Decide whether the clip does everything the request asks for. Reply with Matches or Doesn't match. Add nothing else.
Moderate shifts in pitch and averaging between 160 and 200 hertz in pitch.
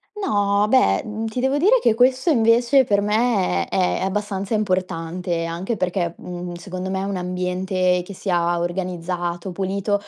Matches